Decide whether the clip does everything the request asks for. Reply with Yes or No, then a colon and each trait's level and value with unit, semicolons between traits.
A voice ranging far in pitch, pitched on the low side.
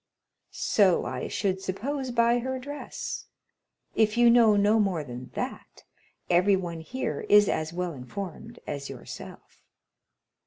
No: wide, 5.8 semitones; high, 200 Hz